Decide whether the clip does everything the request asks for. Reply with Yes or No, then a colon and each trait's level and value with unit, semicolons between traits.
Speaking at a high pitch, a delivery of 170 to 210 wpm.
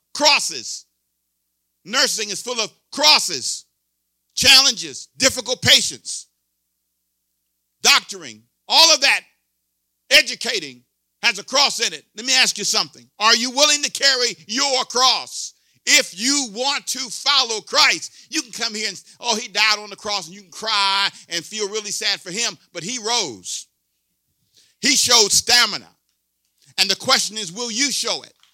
No: high, 205 Hz; average, 150 wpm